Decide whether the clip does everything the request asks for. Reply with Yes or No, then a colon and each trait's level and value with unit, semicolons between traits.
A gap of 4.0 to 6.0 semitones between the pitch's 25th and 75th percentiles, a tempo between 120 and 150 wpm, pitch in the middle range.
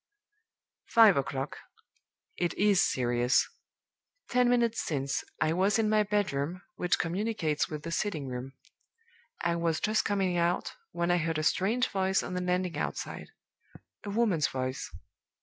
Yes: average, 5.1 semitones; average, 145 wpm; medium, 180 Hz